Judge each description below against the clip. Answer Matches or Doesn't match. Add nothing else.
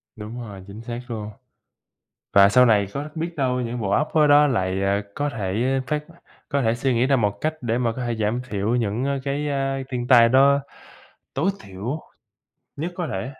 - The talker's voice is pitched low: Matches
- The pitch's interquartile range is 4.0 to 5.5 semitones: Matches